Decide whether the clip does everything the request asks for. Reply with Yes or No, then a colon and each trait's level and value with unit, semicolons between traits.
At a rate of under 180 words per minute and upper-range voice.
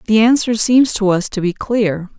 No: fast, 220 wpm; high, 210 Hz